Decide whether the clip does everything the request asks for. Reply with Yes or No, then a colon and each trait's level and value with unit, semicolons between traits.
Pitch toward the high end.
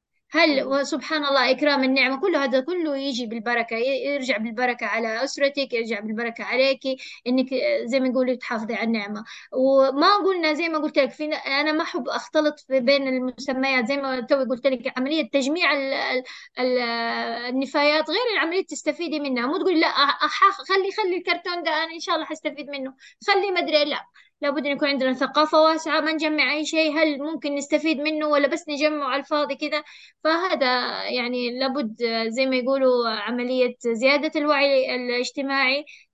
Yes: very high, 280 Hz